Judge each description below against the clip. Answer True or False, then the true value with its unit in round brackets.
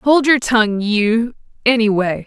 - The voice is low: False (230 Hz)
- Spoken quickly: False (130 wpm)